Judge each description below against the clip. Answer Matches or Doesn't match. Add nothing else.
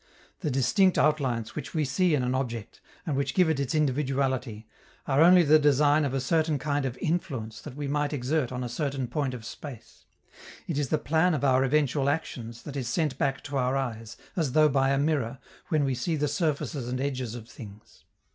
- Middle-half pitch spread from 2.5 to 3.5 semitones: Matches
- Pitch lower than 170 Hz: Matches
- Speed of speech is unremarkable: Doesn't match